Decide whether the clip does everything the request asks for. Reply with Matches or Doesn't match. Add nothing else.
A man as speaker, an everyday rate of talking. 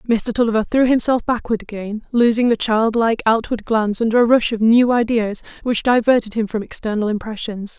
Doesn't match